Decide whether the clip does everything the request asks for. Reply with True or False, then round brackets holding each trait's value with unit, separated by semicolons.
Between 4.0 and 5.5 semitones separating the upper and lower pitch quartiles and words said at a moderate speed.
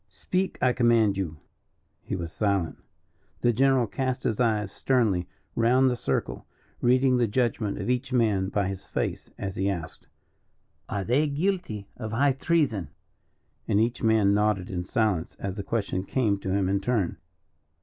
True (4.3 semitones; 160 wpm)